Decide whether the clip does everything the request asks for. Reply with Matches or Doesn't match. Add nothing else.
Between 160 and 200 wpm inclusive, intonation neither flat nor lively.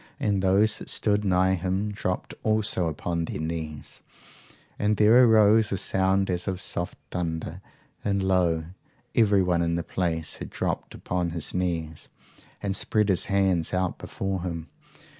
Doesn't match